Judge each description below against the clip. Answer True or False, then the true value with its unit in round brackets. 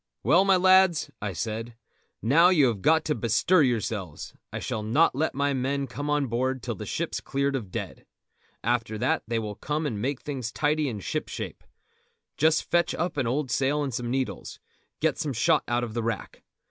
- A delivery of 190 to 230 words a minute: True (195 wpm)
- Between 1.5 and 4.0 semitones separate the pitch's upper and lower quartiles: False (4.5 semitones)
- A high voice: False (130 Hz)